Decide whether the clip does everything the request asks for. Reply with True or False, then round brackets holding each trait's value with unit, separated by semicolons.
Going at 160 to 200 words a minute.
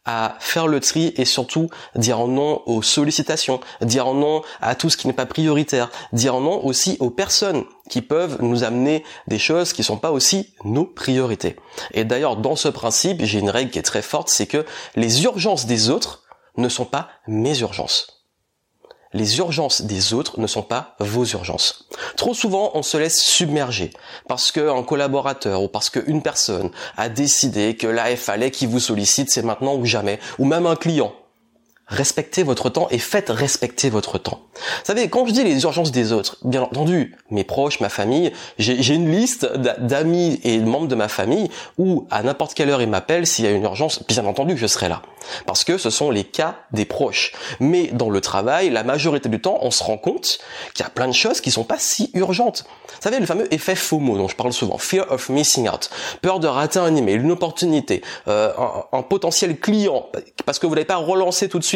False (210 wpm)